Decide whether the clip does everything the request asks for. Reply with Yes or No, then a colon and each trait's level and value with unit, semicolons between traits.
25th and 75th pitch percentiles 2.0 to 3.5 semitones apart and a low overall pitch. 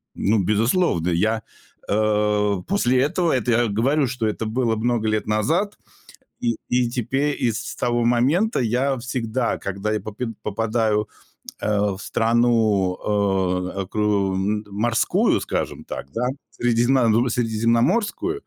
Yes: average, 2.8 semitones; low, 115 Hz